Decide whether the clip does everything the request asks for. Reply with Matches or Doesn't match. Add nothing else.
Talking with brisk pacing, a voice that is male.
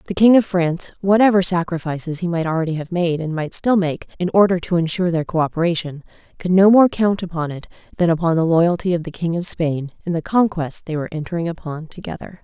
Doesn't match